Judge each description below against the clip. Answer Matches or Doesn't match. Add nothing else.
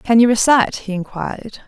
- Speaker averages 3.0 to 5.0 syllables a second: Doesn't match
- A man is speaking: Doesn't match